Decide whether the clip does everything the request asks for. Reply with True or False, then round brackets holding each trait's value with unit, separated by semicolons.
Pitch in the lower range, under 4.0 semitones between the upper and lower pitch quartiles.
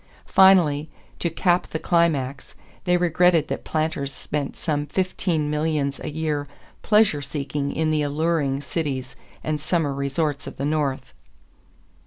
False (150 Hz; 2.7 semitones)